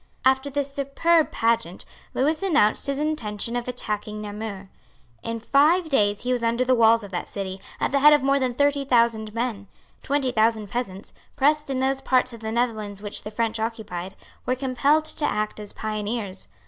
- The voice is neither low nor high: No, high, 235 Hz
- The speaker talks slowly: No, average, 185 wpm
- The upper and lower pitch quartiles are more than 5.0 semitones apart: No, average, 4.6 semitones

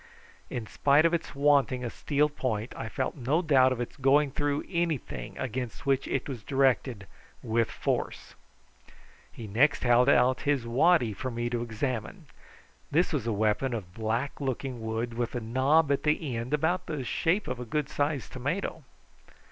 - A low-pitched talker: Yes, low, 130 Hz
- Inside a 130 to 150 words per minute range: No, average, 170 wpm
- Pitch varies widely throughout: No, average, 3.6 semitones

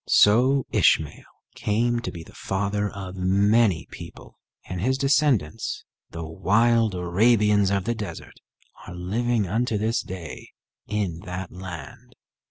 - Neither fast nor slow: No, slow, 130 wpm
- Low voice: Yes, low, 100 Hz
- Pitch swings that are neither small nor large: Yes, average, 4.1 semitones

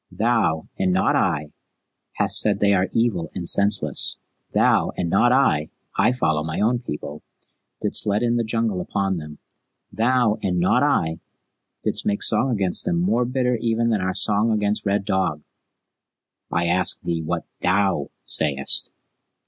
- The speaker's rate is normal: Yes, average, 160 wpm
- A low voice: Yes, low, 100 Hz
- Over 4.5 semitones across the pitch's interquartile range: Yes, average, 5.3 semitones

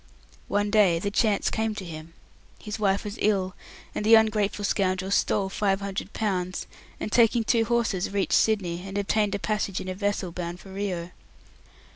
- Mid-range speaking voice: No, high, 200 Hz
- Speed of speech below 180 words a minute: Yes, average, 170 wpm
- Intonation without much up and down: Yes, narrow, 2.3 semitones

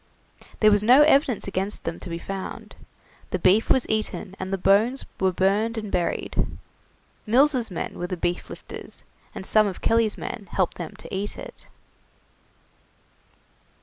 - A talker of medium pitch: No, high, 200 Hz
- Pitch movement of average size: Yes, average, 3.2 semitones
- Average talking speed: Yes, average, 155 wpm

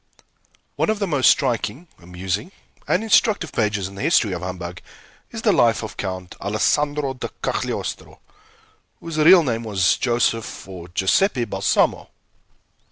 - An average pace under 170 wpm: Yes, average, 140 wpm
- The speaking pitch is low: Yes, low, 115 Hz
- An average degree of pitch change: No, wide, 8.1 semitones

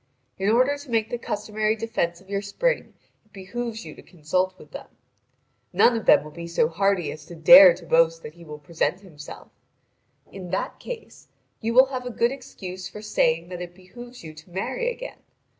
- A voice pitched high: Yes, high, 195 Hz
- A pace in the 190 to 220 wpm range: Yes, average, 200 wpm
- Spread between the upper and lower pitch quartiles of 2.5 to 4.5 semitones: No, average, 5.3 semitones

